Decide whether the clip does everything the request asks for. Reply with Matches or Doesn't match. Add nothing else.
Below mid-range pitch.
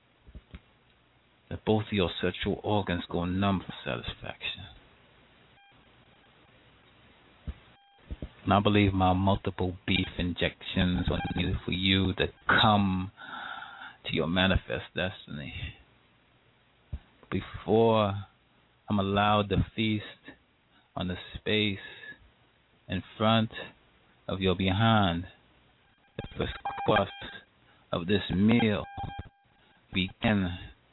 Matches